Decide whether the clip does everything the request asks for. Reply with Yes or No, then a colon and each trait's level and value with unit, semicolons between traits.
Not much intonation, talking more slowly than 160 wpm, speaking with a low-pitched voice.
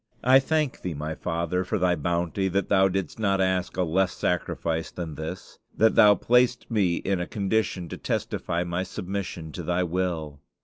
No: narrow, 2.3 semitones; average, 180 wpm; very low, 90 Hz